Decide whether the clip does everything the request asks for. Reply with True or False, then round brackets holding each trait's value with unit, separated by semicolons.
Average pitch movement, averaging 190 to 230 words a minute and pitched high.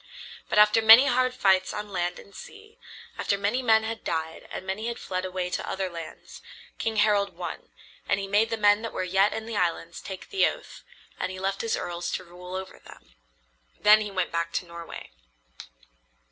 True (3.4 semitones; 200 wpm; 195 Hz)